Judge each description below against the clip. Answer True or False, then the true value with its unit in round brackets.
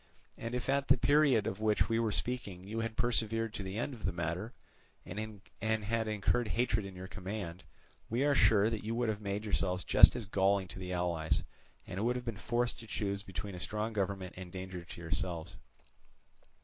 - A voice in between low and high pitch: False (105 Hz)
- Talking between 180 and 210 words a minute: True (200 wpm)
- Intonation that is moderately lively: True (3.4 semitones)